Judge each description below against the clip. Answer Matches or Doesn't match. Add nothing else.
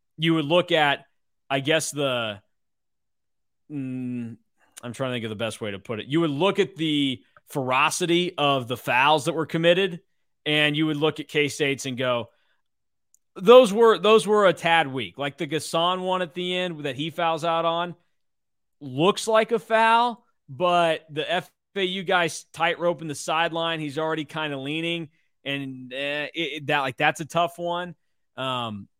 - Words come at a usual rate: Matches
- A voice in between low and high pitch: Matches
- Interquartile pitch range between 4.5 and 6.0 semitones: Doesn't match